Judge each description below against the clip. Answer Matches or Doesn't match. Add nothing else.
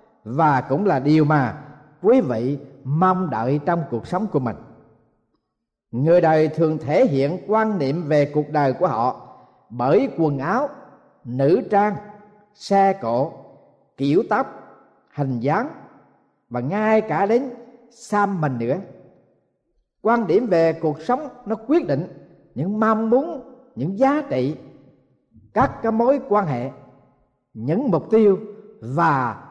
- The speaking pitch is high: Doesn't match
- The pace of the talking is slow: Matches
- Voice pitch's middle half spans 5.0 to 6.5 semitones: Doesn't match